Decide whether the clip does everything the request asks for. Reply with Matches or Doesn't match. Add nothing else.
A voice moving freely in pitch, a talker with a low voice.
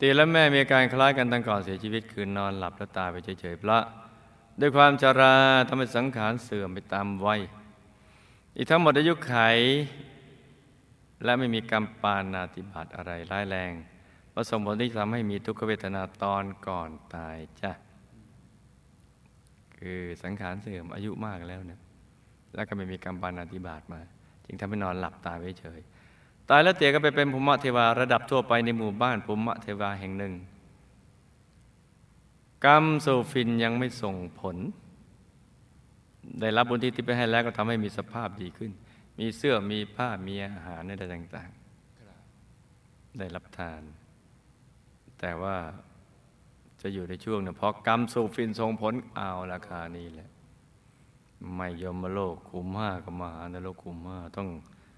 Doesn't match